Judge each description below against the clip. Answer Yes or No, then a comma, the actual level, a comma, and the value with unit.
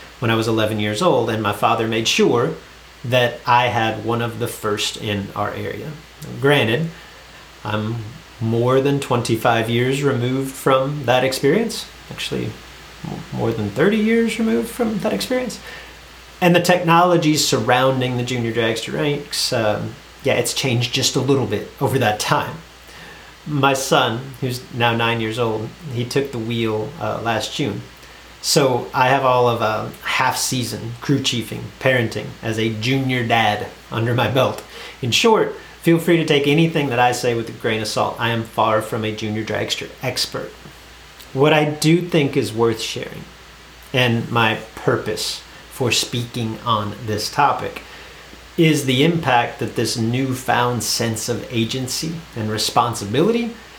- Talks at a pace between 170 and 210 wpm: No, average, 155 wpm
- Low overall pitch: Yes, low, 120 Hz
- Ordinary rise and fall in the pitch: Yes, average, 3.8 semitones